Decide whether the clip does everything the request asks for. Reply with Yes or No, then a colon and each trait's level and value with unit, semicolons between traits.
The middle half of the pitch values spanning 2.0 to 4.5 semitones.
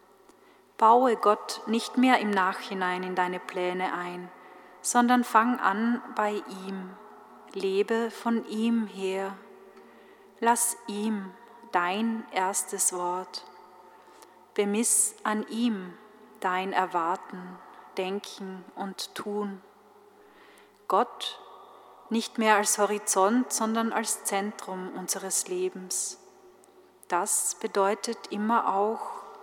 Yes: average, 3.3 semitones